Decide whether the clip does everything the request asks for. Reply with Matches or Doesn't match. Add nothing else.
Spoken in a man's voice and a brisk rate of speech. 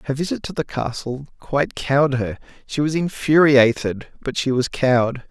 Doesn't match